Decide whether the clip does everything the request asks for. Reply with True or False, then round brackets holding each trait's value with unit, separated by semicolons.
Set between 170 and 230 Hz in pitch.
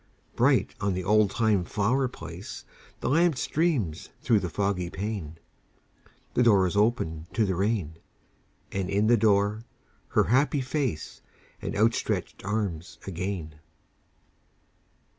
False (105 Hz)